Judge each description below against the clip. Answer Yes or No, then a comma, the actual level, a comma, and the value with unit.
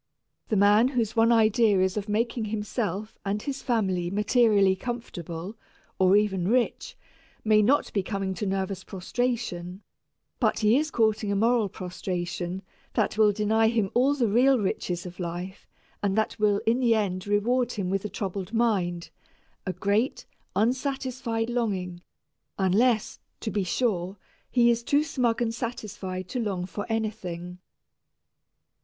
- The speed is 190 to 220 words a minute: No, average, 150 wpm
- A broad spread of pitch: No, average, 3.6 semitones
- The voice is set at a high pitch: Yes, high, 210 Hz